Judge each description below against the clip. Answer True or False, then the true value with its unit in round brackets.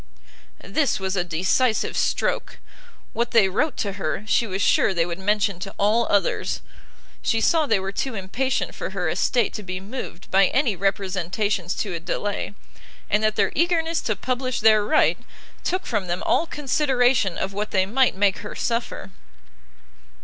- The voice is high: True (210 Hz)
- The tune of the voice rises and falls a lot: False (4.4 semitones)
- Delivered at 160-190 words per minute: True (170 wpm)